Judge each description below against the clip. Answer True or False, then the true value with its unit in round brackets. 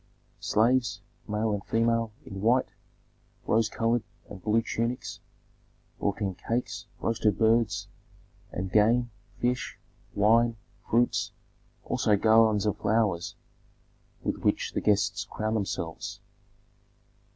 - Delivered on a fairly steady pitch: True (2.0 semitones)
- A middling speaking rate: False (105 wpm)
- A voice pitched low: True (110 Hz)